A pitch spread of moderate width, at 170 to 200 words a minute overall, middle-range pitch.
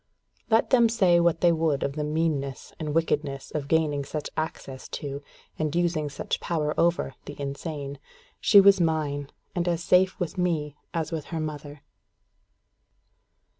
No: average, 3.0 semitones; average, 155 wpm; medium, 155 Hz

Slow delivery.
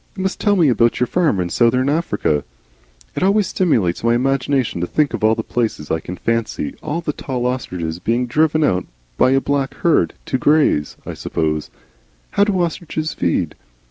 No: average, 180 wpm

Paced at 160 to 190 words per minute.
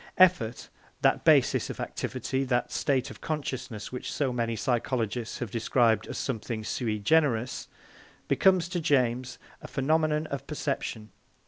No: slow, 135 wpm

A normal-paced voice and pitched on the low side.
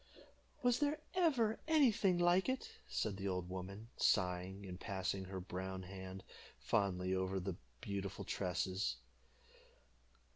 No: slow, 125 wpm; very low, 95 Hz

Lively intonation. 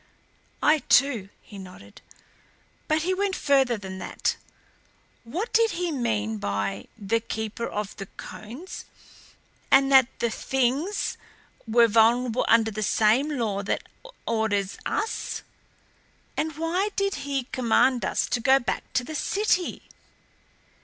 Yes: wide, 6.1 semitones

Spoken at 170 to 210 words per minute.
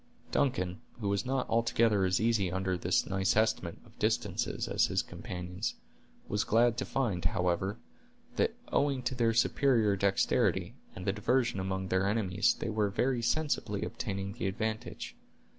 No: average, 155 wpm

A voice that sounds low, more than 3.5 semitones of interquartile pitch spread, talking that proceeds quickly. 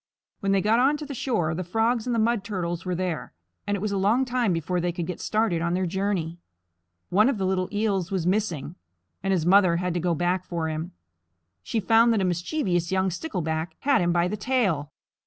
No: medium, 185 Hz; average, 4.0 semitones; fast, 220 wpm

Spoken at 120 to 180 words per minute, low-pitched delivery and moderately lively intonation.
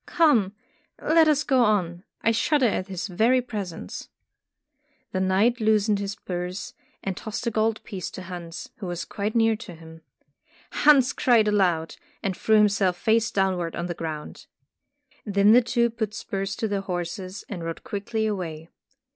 No: average, 165 wpm; high, 200 Hz; average, 3.8 semitones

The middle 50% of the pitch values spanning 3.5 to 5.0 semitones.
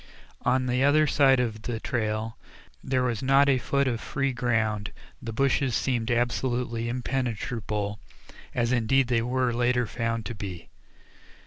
No: narrow, 2.4 semitones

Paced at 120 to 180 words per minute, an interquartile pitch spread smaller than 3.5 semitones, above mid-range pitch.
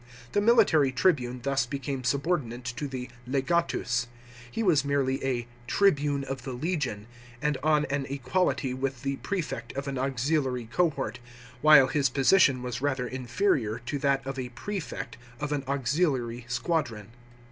No: average, 150 wpm; average, 3.1 semitones; low, 135 Hz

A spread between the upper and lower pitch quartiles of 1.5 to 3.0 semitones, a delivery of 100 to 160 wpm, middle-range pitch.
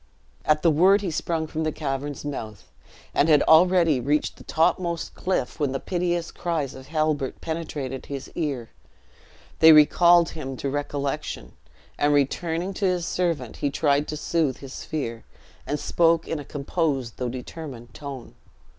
No: average, 3.4 semitones; average, 155 wpm; medium, 150 Hz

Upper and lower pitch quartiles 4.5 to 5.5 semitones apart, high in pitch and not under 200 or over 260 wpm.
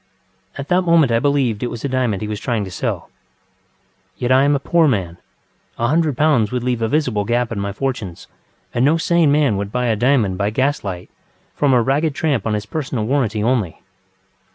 No: average, 5.0 semitones; low, 125 Hz; fast, 205 wpm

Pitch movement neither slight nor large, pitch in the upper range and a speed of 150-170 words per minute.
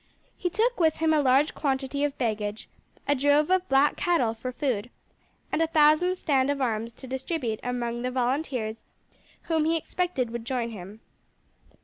Yes: average, 4.8 semitones; very high, 270 Hz; average, 165 wpm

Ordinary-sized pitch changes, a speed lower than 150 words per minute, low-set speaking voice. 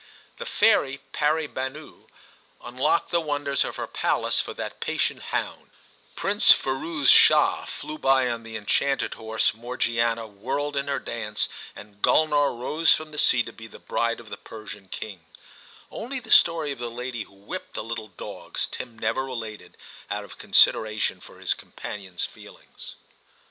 No: average, 4.7 semitones; average, 160 wpm; low, 120 Hz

